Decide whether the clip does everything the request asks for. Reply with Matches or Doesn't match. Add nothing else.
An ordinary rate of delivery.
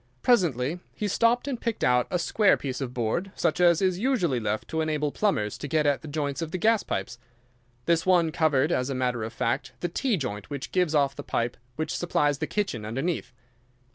Doesn't match